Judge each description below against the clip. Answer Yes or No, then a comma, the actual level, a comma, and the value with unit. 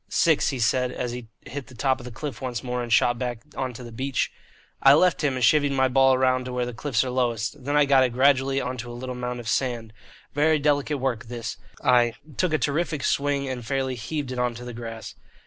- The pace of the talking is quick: Yes, fast, 240 wpm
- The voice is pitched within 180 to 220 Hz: No, low, 130 Hz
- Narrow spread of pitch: Yes, narrow, 2.3 semitones